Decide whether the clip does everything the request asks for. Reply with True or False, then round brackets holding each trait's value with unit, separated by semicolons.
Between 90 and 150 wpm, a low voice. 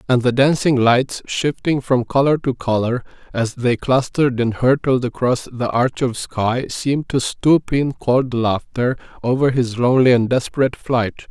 False (165 wpm; 125 Hz)